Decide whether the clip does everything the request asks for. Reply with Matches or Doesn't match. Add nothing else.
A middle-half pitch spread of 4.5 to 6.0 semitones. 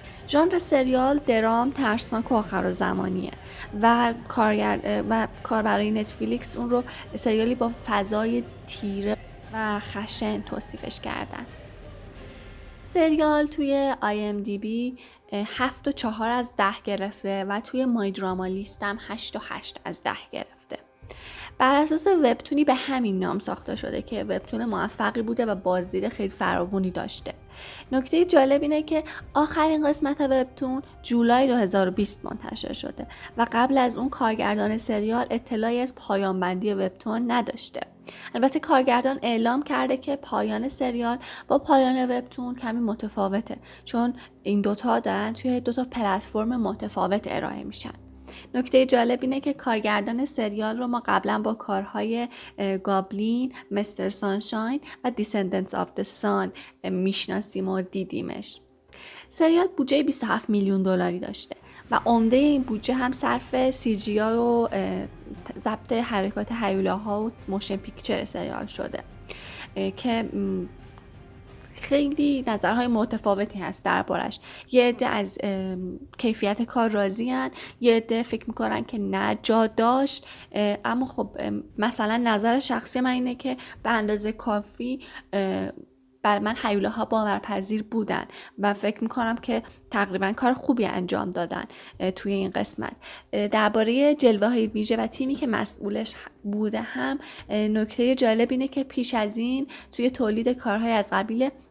Doesn't match